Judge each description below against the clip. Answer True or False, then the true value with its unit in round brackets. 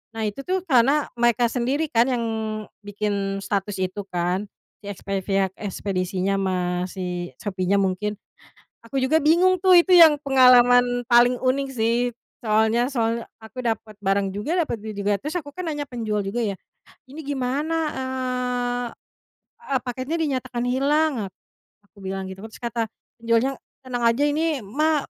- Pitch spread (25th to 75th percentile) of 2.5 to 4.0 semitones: False (5.0 semitones)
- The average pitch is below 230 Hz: False (240 Hz)